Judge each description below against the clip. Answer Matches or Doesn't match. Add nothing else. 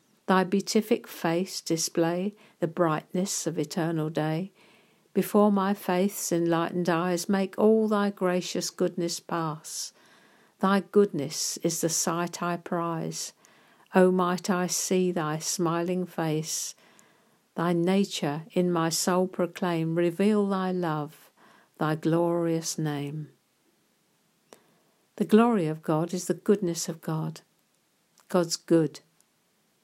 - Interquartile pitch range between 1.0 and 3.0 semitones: Matches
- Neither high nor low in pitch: Matches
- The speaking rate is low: Matches